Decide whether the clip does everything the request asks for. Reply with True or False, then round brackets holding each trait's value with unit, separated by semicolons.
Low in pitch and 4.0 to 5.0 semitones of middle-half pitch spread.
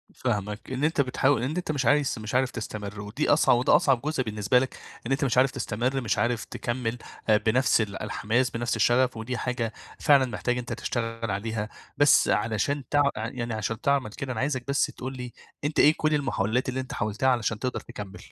False (125 Hz; 3.2 semitones)